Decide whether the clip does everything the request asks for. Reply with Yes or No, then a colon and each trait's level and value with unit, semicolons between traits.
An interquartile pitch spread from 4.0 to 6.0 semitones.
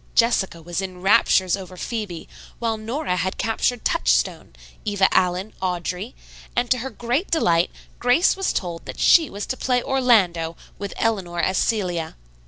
Yes: average, 5.2 semitones